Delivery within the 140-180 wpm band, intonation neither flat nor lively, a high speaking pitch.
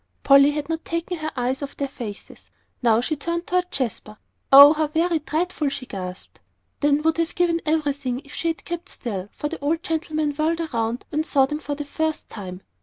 No: average, 200 wpm; average, 3.4 semitones; very high, 295 Hz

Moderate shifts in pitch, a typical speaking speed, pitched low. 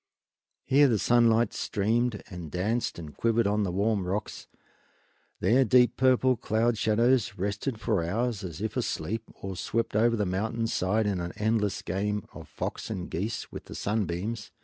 Yes: average, 3.1 semitones; average, 165 wpm; low, 110 Hz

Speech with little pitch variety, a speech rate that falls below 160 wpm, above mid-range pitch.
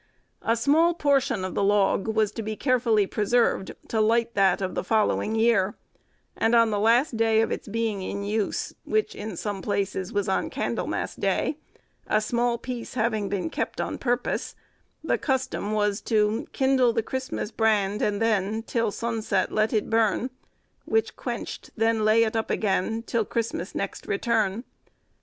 No: narrow, 2.3 semitones; average, 170 wpm; high, 220 Hz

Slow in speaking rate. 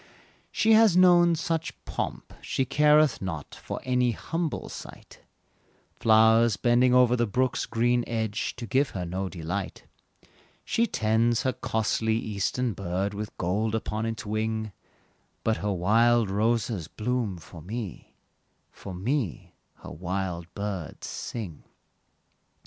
Yes: slow, 125 wpm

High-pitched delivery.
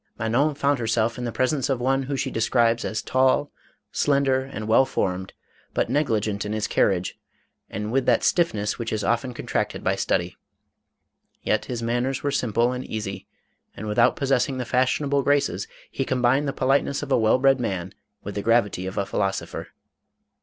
No: low, 120 Hz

